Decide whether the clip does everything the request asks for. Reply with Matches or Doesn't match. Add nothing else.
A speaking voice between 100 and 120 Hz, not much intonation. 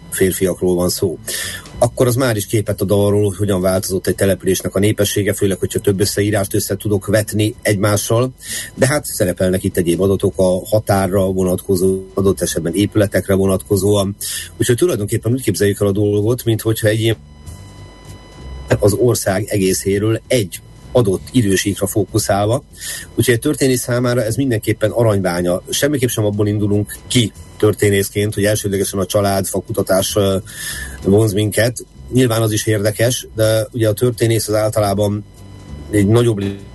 Matches